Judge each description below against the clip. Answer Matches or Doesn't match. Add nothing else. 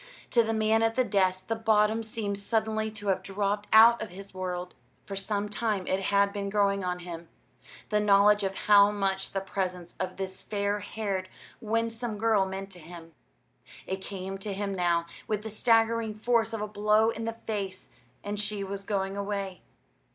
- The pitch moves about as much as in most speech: Doesn't match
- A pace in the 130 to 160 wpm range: Doesn't match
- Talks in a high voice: Matches